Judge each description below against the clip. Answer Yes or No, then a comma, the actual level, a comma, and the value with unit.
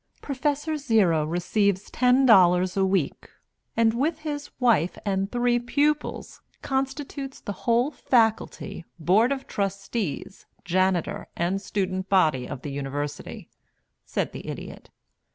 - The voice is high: Yes, high, 200 Hz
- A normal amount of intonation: No, wide, 6.0 semitones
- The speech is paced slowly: Yes, slow, 120 wpm